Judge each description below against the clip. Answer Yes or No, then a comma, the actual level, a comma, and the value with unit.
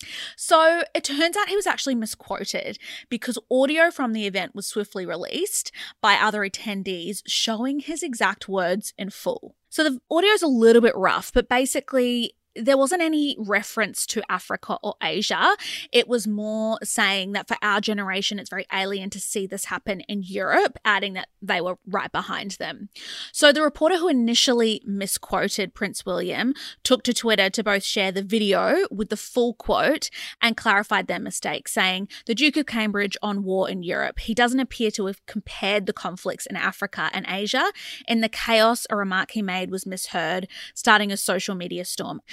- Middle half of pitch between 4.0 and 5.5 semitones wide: Yes, average, 4.6 semitones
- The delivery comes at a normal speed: Yes, average, 180 wpm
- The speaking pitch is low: No, high, 215 Hz